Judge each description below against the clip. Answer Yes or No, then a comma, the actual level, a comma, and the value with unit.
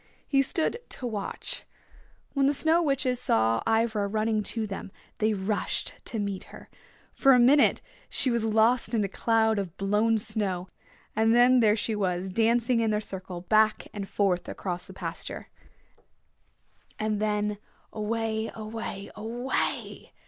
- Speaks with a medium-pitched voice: No, high, 220 Hz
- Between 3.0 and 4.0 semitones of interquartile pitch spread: No, narrow, 2.5 semitones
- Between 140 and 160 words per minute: Yes, average, 150 wpm